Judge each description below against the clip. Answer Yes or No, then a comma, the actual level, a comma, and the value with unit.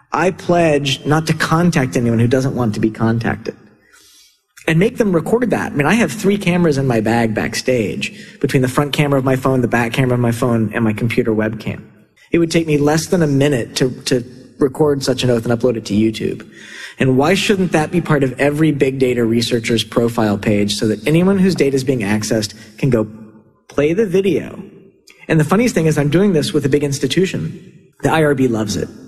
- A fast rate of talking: Yes, fast, 215 wpm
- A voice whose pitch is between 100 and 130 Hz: No, medium, 140 Hz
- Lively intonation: Yes, wide, 5.7 semitones